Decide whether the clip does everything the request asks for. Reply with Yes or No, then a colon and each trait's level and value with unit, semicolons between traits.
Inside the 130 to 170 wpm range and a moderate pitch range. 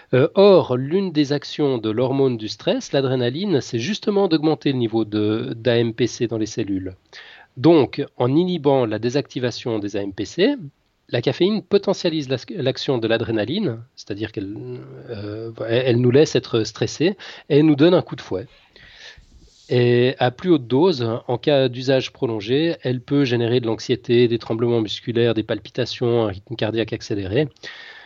Yes: average, 150 wpm; average, 4.4 semitones